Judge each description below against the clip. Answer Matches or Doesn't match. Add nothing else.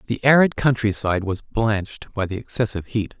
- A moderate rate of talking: Matches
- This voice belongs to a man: Matches